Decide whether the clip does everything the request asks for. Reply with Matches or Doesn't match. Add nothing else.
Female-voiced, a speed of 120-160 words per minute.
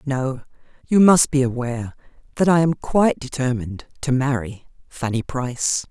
Matches